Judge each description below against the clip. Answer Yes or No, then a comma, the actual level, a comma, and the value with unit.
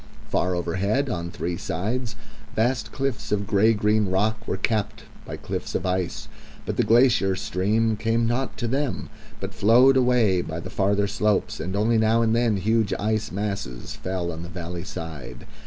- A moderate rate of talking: Yes, average, 170 wpm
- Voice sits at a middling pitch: No, low, 105 Hz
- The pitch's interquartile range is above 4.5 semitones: No, average, 3.6 semitones